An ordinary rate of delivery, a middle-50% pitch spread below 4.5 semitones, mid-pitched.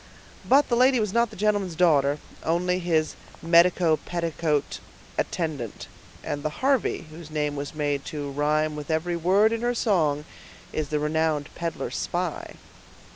Yes: average, 150 wpm; average, 3.5 semitones; medium, 160 Hz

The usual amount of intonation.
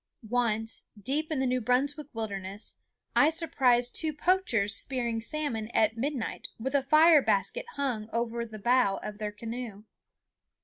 Yes: average, 4.3 semitones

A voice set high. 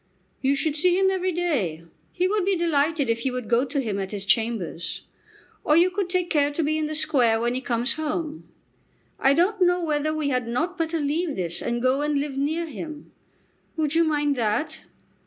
Yes: very high, 295 Hz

